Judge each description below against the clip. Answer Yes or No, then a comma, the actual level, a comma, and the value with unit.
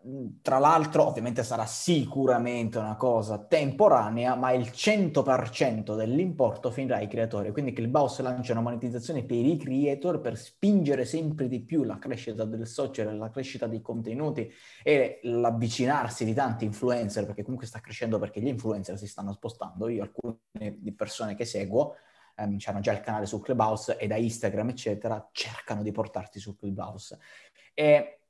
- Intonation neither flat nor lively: Yes, average, 3.2 semitones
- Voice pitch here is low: Yes, low, 120 Hz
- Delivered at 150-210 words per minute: Yes, average, 155 wpm